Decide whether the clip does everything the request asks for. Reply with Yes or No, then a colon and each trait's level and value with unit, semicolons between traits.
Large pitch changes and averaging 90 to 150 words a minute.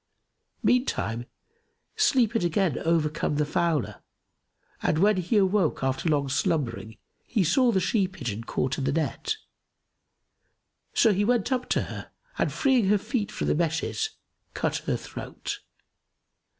Yes: wide, 6.9 semitones; average, 140 wpm